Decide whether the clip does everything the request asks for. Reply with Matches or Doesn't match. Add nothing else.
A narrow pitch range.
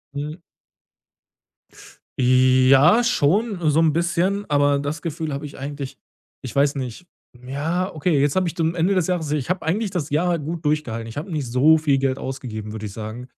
Doesn't match